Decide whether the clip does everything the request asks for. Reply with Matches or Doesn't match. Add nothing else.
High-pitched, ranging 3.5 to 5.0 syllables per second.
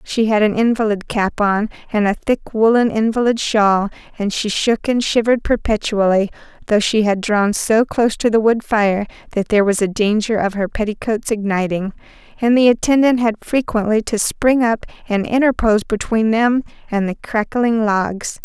Matches